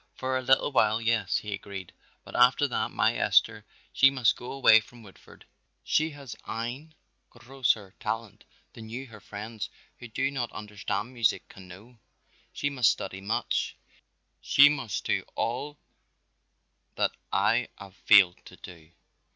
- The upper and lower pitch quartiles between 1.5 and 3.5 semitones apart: No, average, 4.2 semitones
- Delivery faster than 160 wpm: No, average, 150 wpm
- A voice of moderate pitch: No, low, 115 Hz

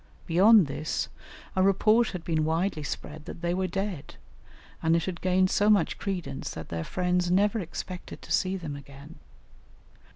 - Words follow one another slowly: No, average, 165 wpm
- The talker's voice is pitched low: No, medium, 180 Hz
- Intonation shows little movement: No, average, 3.4 semitones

